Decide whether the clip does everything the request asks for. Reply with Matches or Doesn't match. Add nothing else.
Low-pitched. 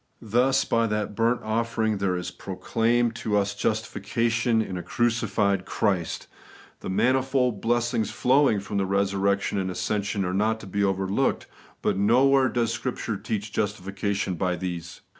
Matches